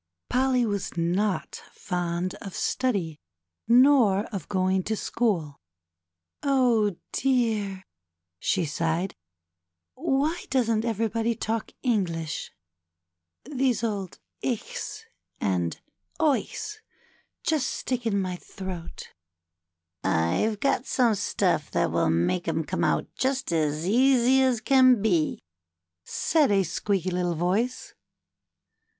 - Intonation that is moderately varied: No, wide, 6.2 semitones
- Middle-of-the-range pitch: No, high, 210 Hz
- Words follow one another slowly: Yes, slow, 110 wpm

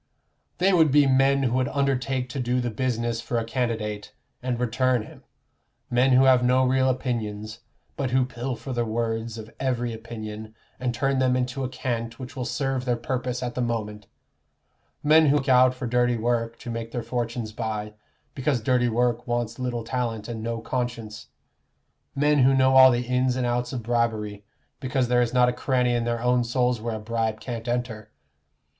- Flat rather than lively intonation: Yes, narrow, 1.9 semitones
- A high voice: No, low, 120 Hz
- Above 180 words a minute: Yes, average, 190 wpm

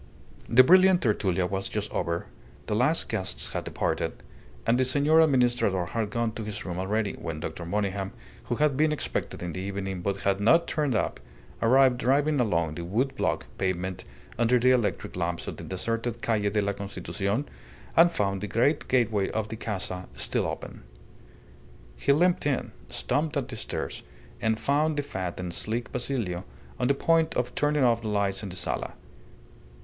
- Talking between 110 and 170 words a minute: No, average, 180 wpm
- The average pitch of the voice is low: Yes, low, 110 Hz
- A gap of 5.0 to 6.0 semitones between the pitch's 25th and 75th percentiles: Yes, wide, 5.5 semitones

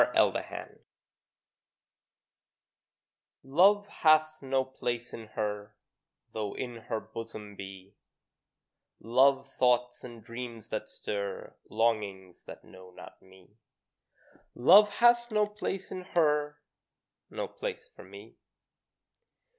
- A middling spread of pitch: No, wide, 6.8 semitones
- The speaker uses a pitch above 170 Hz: No, low, 120 Hz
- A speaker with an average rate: No, slow, 105 wpm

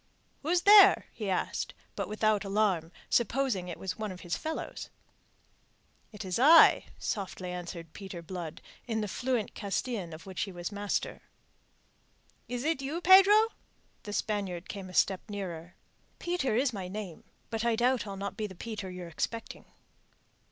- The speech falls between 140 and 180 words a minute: Yes, average, 155 wpm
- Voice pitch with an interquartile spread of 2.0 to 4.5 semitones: No, average, 5.1 semitones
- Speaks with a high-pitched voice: Yes, high, 205 Hz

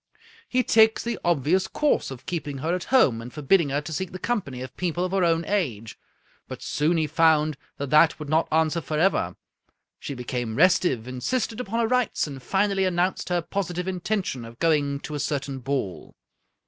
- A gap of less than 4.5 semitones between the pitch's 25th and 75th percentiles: No, average, 5.2 semitones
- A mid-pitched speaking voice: Yes, medium, 160 Hz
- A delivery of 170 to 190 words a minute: Yes, average, 185 wpm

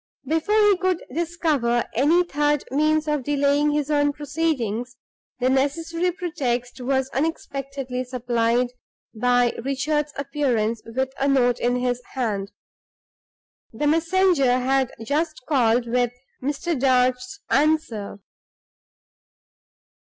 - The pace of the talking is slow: Yes, slow, 110 wpm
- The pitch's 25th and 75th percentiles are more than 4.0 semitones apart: No, average, 3.7 semitones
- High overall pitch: Yes, very high, 275 Hz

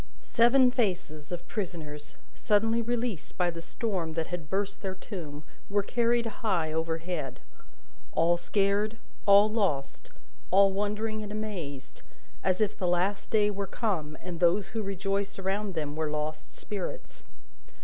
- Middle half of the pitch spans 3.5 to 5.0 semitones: Yes, average, 4.2 semitones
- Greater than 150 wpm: No, average, 140 wpm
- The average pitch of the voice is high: Yes, high, 195 Hz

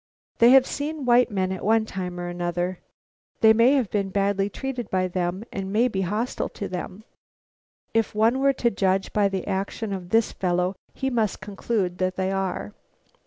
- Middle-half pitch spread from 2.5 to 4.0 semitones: Yes, average, 3.6 semitones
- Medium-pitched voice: No, high, 200 Hz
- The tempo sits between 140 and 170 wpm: No, average, 185 wpm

